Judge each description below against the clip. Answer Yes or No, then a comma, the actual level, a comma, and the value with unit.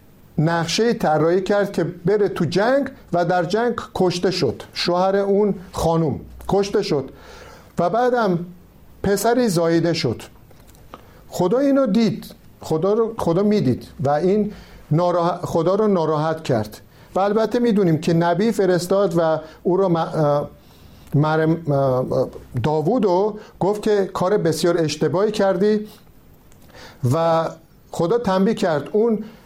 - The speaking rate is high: No, average, 120 wpm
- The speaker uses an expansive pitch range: No, average, 4.5 semitones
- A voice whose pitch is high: No, medium, 180 Hz